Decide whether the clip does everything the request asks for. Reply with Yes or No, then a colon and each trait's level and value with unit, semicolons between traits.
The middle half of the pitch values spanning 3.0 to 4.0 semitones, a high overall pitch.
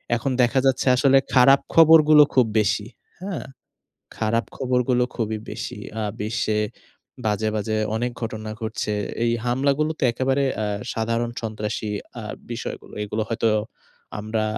No: average, 3.5 semitones; low, 115 Hz